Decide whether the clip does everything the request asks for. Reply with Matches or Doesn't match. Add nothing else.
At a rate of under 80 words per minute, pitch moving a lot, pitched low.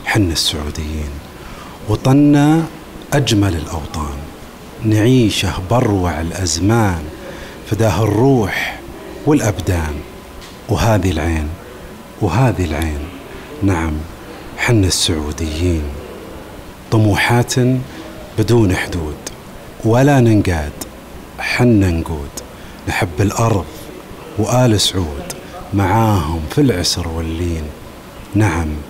Matches